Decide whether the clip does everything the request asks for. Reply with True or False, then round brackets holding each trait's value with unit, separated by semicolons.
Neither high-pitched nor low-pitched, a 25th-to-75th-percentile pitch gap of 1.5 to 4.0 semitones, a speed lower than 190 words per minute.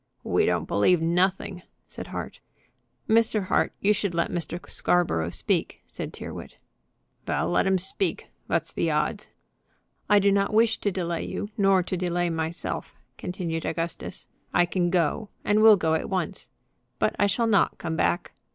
True (180 Hz; 3.1 semitones; 160 wpm)